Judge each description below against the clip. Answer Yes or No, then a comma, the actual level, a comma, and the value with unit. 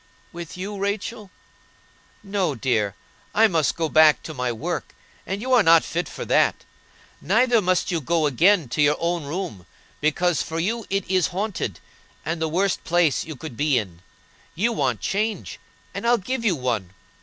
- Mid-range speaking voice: Yes, medium, 170 Hz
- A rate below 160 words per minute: No, average, 175 wpm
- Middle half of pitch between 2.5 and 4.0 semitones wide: No, average, 5.1 semitones